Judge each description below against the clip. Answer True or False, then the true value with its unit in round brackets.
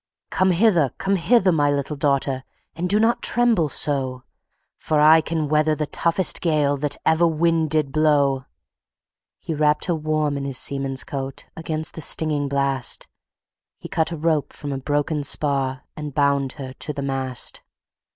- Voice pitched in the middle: True (150 Hz)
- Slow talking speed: False (165 wpm)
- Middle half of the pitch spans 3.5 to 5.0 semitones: False (2.6 semitones)